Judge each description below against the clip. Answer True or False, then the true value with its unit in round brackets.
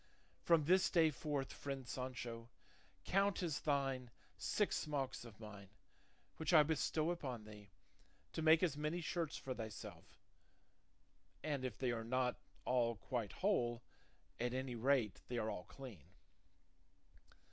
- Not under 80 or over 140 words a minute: True (135 wpm)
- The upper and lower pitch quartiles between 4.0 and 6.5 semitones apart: True (4.7 semitones)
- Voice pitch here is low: True (130 Hz)